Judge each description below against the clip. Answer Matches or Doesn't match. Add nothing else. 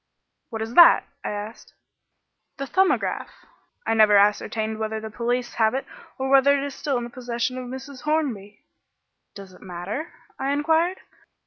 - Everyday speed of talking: Matches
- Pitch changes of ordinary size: Matches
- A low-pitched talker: Doesn't match